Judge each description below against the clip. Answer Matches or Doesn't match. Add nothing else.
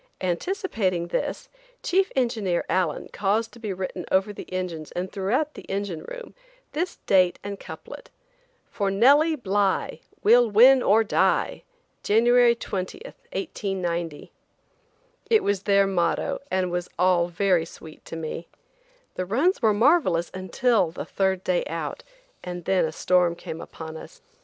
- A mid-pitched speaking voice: Doesn't match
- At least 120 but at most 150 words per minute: Matches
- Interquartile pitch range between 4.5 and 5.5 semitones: Matches